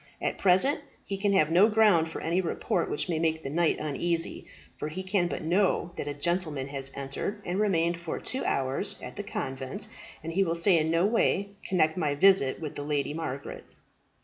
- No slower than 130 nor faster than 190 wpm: No, average, 200 wpm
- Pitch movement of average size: Yes, average, 4.2 semitones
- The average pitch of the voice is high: No, medium, 165 Hz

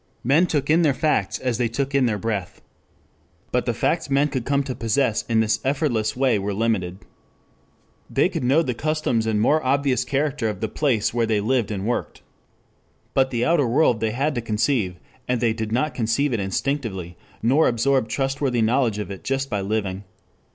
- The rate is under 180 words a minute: No, average, 195 wpm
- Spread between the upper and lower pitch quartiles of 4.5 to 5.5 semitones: No, average, 4.0 semitones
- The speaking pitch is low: Yes, low, 120 Hz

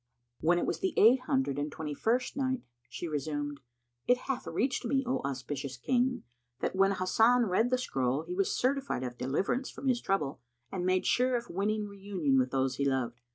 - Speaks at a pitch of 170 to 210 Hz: Yes, high, 190 Hz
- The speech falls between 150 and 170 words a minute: No, average, 195 wpm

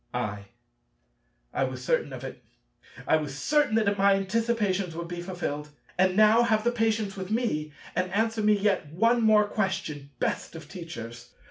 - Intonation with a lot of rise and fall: Yes, wide, 5.7 semitones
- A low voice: No, high, 190 Hz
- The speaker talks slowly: No, average, 160 wpm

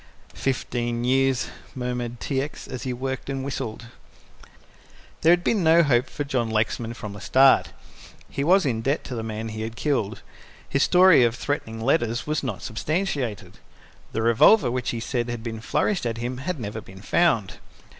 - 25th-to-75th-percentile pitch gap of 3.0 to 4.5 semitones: Yes, average, 3.6 semitones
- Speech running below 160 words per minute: No, average, 175 wpm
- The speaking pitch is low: Yes, low, 125 Hz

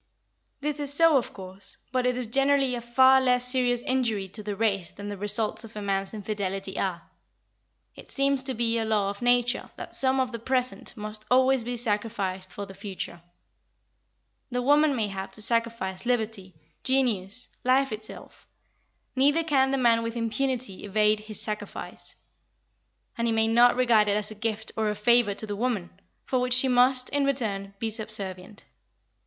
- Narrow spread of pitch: No, average, 3.6 semitones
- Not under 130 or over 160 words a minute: No, average, 180 wpm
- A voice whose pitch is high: Yes, high, 230 Hz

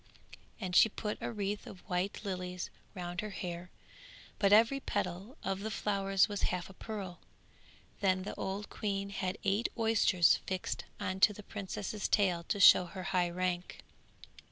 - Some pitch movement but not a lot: No, narrow, 2.2 semitones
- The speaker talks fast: No, average, 160 wpm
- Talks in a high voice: Yes, high, 195 Hz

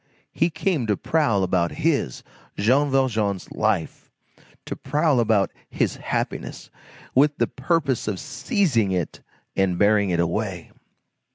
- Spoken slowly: Yes, slow, 125 wpm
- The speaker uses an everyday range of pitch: No, wide, 7.0 semitones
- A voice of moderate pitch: No, low, 115 Hz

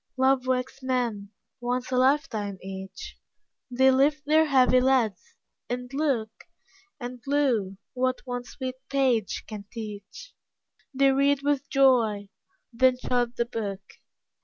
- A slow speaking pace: Yes, slow, 125 wpm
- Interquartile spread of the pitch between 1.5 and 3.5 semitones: Yes, average, 3.1 semitones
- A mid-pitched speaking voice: No, very high, 255 Hz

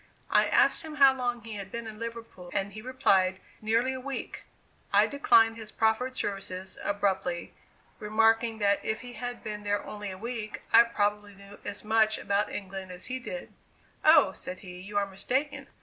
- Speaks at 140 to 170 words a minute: No, average, 180 wpm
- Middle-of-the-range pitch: No, high, 215 Hz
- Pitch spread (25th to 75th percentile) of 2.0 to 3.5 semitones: Yes, average, 3.0 semitones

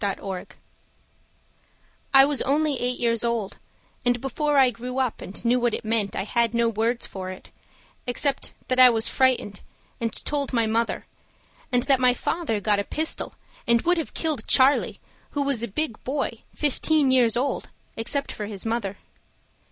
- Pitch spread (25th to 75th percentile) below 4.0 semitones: Yes, average, 3.4 semitones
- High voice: Yes, high, 245 Hz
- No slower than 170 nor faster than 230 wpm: Yes, average, 175 wpm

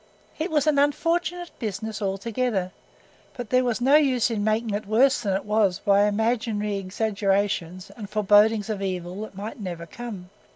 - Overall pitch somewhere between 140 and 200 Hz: No, high, 215 Hz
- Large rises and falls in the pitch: No, average, 3.5 semitones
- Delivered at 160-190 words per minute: Yes, average, 165 wpm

